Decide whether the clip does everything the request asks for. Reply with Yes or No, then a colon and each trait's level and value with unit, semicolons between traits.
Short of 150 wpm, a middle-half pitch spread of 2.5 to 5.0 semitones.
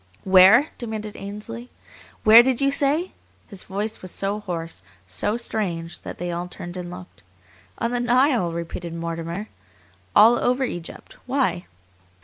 No: average, 140 wpm; wide, 5.5 semitones